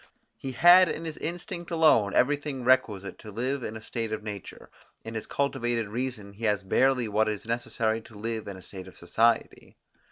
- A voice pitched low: Yes, low, 115 Hz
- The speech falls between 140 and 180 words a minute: No, average, 190 wpm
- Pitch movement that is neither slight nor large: Yes, average, 4.0 semitones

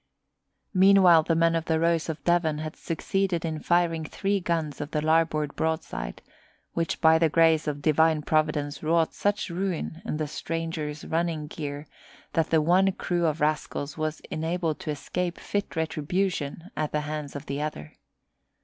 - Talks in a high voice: No, medium, 160 Hz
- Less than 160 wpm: No, average, 165 wpm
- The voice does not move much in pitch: Yes, narrow, 1.9 semitones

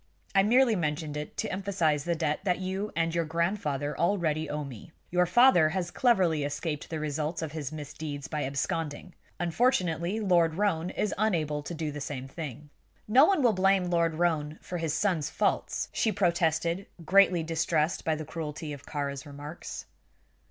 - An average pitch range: Yes, average, 3.5 semitones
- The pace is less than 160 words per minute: No, average, 170 wpm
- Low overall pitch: No, medium, 165 Hz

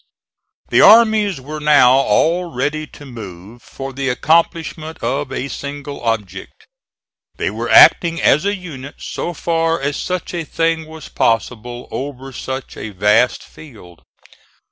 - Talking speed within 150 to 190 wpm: No, average, 140 wpm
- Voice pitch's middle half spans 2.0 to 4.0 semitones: No, average, 4.8 semitones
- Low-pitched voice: No, medium, 145 Hz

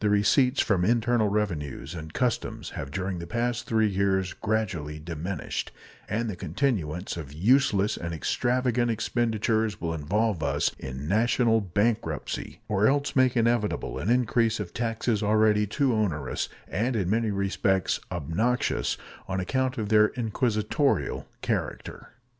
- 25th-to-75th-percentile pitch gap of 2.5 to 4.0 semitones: No, average, 4.6 semitones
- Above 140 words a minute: No, slow, 135 wpm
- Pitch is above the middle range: No, low, 105 Hz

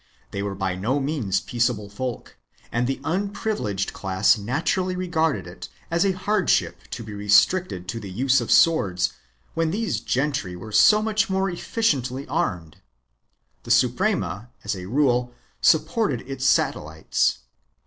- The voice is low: Yes, low, 125 Hz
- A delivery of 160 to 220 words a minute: No, average, 140 wpm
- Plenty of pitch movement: Yes, wide, 8.7 semitones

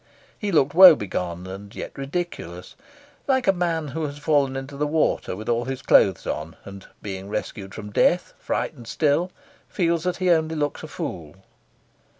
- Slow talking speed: No, average, 165 wpm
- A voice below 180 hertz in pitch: Yes, medium, 140 Hz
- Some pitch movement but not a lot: No, wide, 8.4 semitones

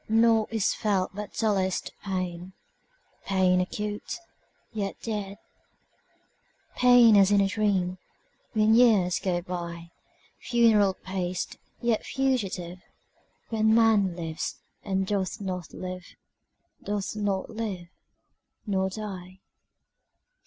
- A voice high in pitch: Yes, high, 195 Hz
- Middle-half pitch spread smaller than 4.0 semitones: Yes, average, 2.9 semitones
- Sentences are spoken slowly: Yes, slow, 80 wpm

